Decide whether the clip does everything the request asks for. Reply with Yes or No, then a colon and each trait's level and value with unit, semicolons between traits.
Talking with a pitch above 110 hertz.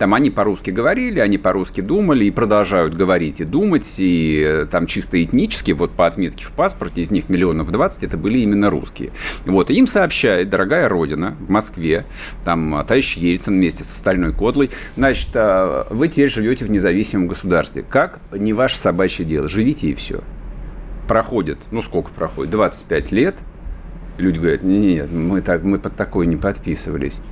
No: very low, 95 Hz